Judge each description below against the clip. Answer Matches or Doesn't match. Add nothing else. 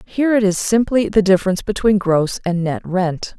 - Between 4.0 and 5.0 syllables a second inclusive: Doesn't match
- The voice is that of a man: Doesn't match